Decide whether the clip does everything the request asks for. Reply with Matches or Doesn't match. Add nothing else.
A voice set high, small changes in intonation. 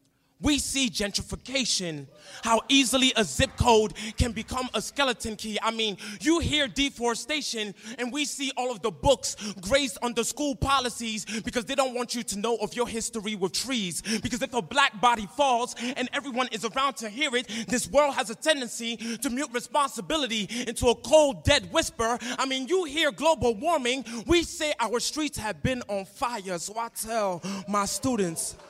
Doesn't match